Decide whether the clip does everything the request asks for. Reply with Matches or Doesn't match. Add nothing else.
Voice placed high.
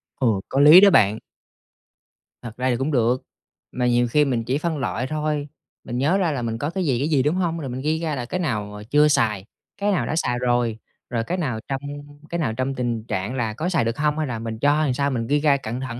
Doesn't match